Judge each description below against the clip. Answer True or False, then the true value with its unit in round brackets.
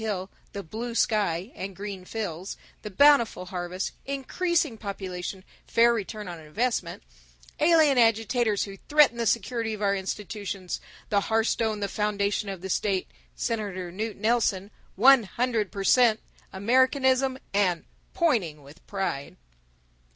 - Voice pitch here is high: True (210 Hz)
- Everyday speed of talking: False (130 wpm)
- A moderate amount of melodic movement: True (3.8 semitones)